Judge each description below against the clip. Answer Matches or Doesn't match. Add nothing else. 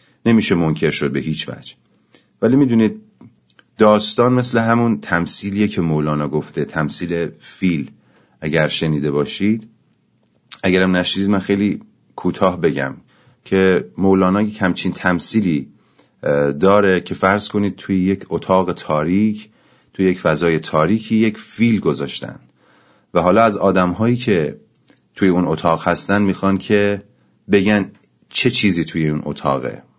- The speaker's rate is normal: Matches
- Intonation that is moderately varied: Matches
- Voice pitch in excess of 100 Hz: Doesn't match